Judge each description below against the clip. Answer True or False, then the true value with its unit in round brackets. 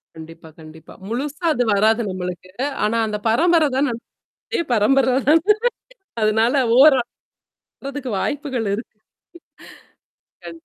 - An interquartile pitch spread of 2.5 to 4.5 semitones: False (5.3 semitones)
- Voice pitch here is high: True (245 Hz)